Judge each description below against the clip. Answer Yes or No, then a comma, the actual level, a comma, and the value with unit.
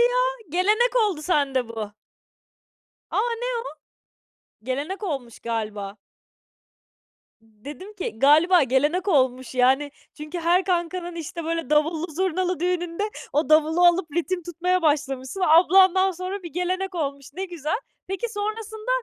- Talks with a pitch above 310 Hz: Yes, very high, 340 Hz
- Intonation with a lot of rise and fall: No, average, 4.7 semitones